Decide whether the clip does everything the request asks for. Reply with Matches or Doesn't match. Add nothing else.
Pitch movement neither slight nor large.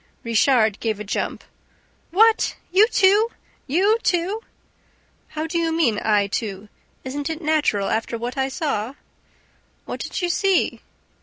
Doesn't match